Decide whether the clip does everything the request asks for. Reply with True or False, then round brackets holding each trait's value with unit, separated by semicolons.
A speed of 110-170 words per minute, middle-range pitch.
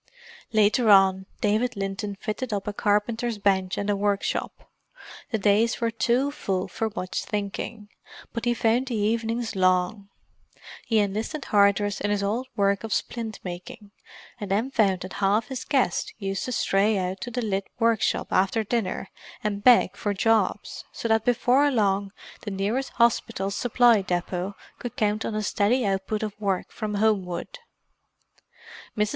False (160 wpm; 210 Hz)